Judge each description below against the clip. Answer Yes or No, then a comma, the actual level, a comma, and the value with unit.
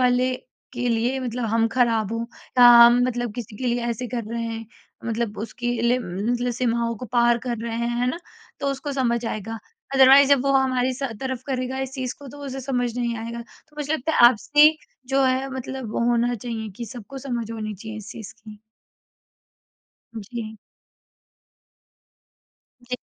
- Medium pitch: No, high, 240 Hz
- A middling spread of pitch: No, narrow, 2.1 semitones